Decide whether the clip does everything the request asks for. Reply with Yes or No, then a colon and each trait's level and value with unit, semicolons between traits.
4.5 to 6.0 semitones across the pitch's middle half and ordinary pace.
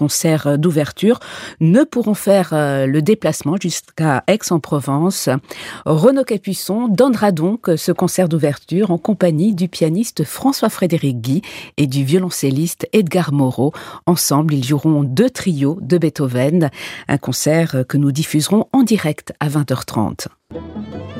No: average, 4.8 semitones; slow, 125 wpm